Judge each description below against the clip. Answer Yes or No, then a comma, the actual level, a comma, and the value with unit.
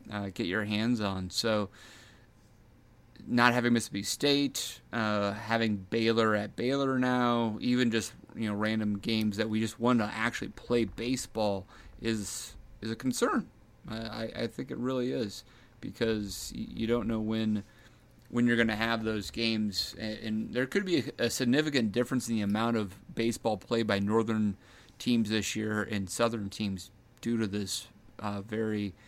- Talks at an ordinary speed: Yes, average, 160 wpm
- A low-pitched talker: Yes, low, 110 Hz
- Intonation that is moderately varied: No, narrow, 2.0 semitones